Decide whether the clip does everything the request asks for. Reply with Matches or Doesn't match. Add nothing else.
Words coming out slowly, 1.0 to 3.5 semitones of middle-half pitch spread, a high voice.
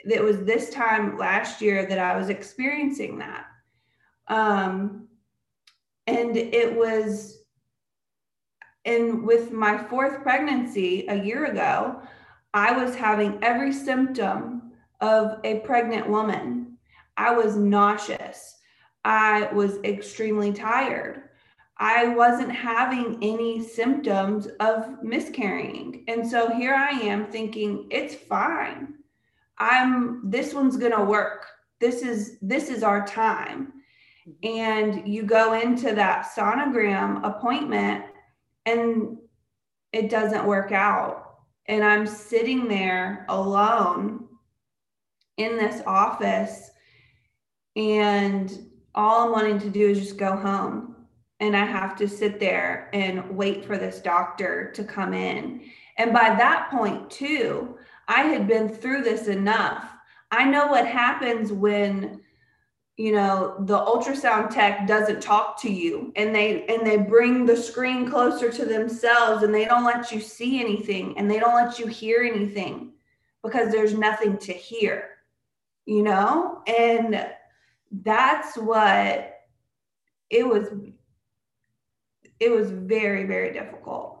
Matches